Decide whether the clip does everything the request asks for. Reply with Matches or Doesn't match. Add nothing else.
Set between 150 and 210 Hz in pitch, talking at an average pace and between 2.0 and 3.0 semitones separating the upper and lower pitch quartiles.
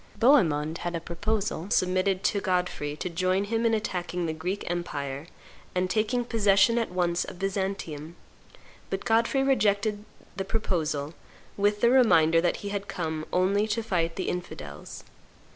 Doesn't match